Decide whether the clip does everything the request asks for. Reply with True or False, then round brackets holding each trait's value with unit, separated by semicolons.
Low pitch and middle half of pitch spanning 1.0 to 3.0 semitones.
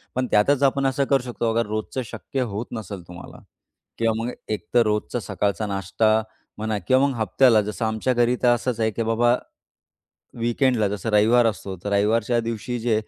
True (115 Hz; 2.5 semitones)